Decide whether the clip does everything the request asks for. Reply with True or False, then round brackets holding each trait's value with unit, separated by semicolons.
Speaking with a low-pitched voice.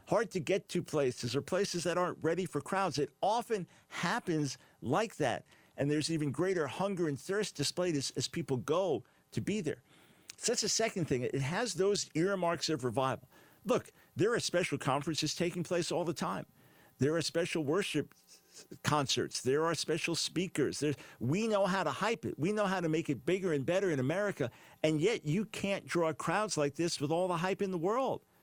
False (170 Hz)